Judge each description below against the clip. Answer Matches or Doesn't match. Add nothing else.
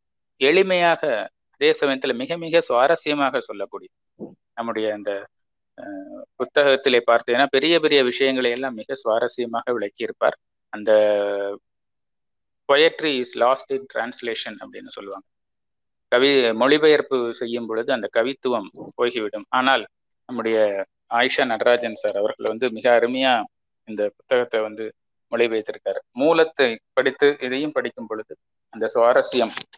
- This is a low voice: Matches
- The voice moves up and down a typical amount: Doesn't match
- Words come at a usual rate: Matches